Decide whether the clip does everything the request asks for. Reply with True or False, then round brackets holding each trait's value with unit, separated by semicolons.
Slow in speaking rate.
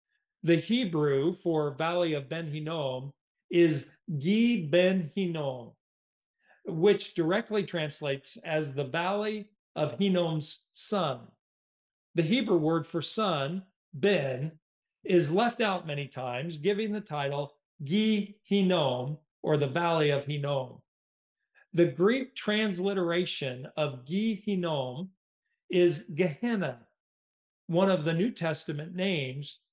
True (110 wpm)